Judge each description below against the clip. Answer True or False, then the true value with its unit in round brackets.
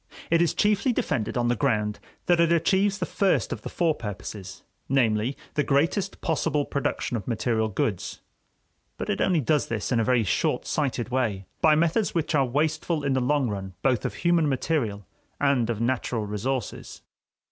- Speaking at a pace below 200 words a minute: True (180 wpm)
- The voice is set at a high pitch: False (135 Hz)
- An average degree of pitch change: False (6.0 semitones)